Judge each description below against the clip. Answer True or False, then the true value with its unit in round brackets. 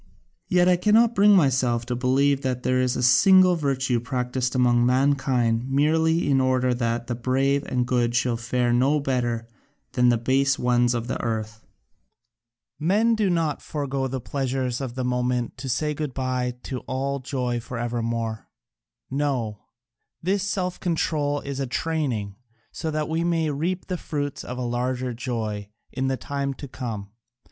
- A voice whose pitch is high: False (130 Hz)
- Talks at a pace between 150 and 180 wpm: True (165 wpm)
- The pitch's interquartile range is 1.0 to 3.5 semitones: True (3.0 semitones)